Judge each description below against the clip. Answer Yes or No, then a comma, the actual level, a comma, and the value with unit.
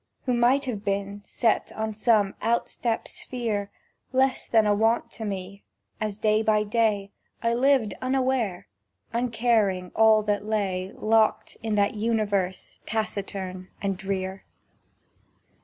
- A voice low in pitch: No, high, 215 Hz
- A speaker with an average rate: No, slow, 125 wpm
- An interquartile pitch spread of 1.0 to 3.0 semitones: Yes, narrow, 2.5 semitones